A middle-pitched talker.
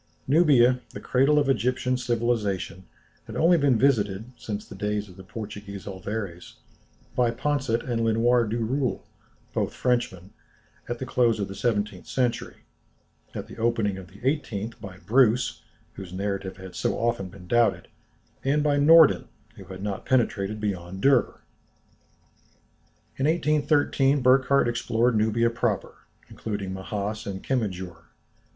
No: low, 115 Hz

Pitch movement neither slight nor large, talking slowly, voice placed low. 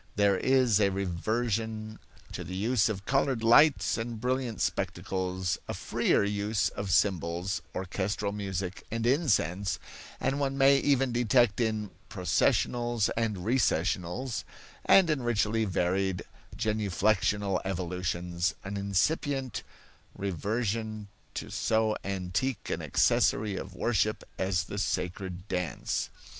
Yes: average, 3.9 semitones; slow, 115 wpm; low, 105 Hz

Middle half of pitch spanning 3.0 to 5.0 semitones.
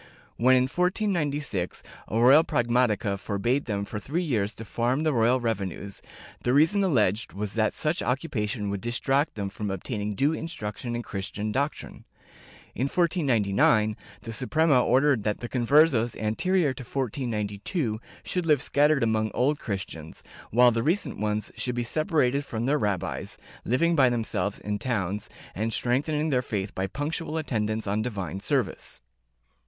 No: wide, 5.4 semitones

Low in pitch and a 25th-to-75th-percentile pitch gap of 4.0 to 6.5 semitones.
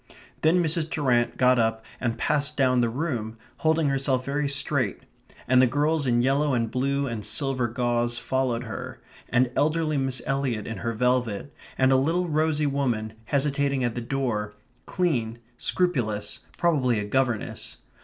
No: low, 130 Hz; average, 3.3 semitones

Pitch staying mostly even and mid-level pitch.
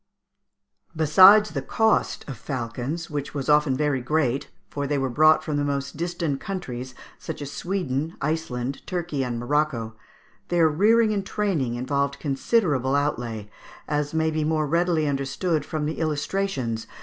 No: average, 3.5 semitones; medium, 150 Hz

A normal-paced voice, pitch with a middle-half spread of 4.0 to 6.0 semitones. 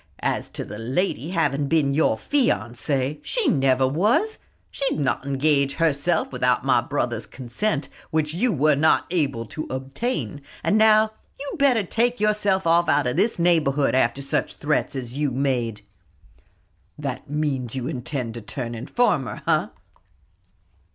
Yes: average, 150 wpm; wide, 5.6 semitones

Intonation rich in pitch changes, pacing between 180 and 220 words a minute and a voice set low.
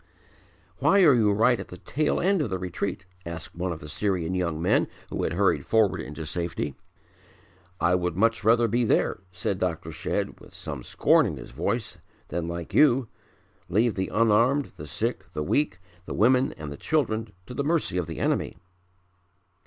Yes: wide, 5.7 semitones; average, 185 wpm; low, 100 Hz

